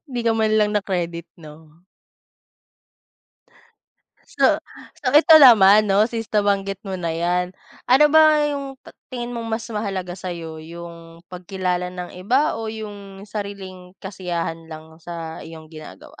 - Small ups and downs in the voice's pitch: No, average, 4.3 semitones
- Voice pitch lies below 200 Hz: Yes, high, 190 Hz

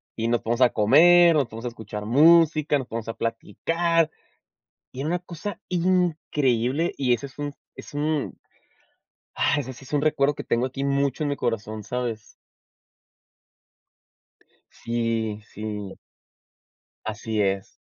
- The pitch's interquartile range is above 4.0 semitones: Yes, average, 5.2 semitones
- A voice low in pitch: Yes, low, 130 Hz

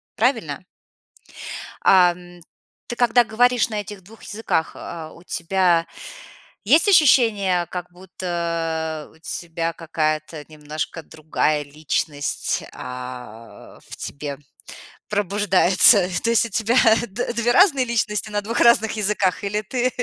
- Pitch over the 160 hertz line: Yes, medium, 185 Hz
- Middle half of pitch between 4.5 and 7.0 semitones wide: Yes, wide, 5.5 semitones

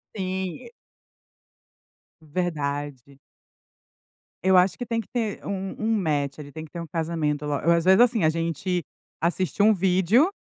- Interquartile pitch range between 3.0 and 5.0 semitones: Yes, average, 3.8 semitones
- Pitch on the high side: No, medium, 175 Hz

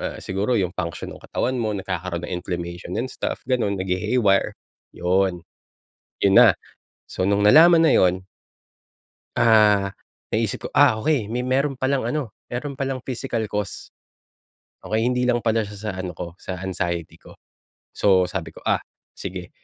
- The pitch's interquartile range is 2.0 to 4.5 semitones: No, average, 5.1 semitones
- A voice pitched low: Yes, low, 105 Hz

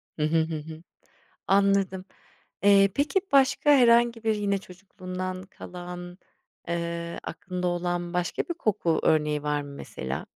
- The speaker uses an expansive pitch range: No, average, 2.9 semitones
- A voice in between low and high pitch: Yes, medium, 180 Hz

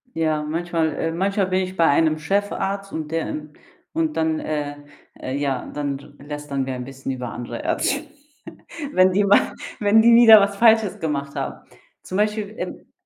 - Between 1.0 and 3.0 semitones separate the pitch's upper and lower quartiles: No, wide, 5.5 semitones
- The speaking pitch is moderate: Yes, medium, 165 Hz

